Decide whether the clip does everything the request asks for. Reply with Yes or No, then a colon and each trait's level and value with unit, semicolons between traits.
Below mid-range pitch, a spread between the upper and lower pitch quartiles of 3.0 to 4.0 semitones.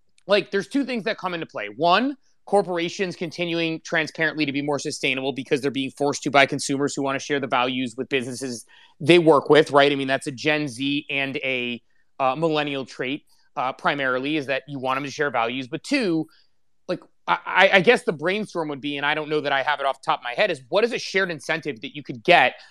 No: medium, 145 Hz; average, 3.6 semitones